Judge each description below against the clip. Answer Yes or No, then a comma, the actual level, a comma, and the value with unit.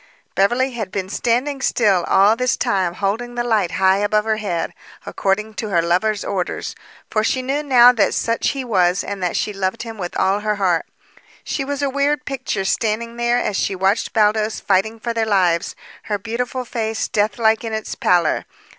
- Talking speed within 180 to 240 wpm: Yes, average, 190 wpm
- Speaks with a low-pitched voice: No, high, 215 Hz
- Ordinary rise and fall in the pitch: Yes, average, 3.6 semitones